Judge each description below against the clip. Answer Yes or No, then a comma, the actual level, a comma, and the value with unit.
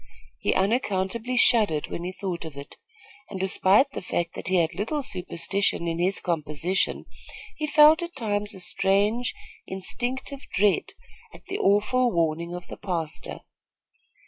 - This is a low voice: No, high, 195 Hz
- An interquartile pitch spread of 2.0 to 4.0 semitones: No, wide, 5.4 semitones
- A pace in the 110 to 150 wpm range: Yes, average, 145 wpm